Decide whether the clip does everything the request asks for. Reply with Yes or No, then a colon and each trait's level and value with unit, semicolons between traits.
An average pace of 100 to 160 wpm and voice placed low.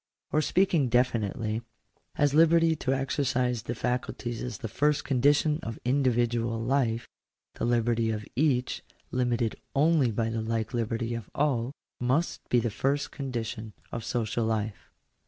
Yes: average, 140 wpm; low, 120 Hz